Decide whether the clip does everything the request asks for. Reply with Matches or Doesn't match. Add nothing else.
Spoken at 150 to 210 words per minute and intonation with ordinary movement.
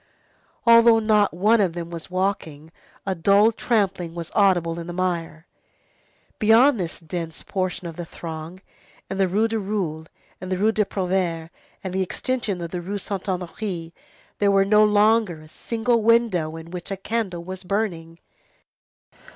Matches